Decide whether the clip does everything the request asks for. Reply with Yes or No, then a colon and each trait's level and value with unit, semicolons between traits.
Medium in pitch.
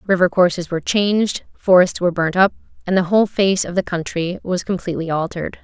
Yes: medium, 180 Hz